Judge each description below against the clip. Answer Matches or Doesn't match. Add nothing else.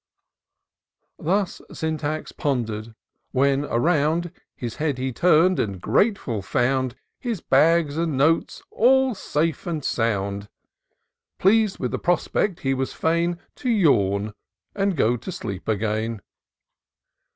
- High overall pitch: Doesn't match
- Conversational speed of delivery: Doesn't match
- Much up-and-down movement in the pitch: Matches